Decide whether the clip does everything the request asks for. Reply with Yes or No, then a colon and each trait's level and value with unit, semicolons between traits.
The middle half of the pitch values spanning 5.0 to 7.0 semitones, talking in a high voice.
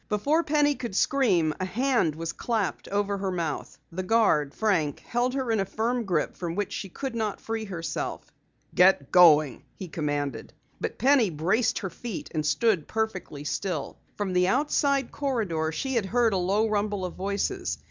Yes: wide, 5.5 semitones; high, 200 Hz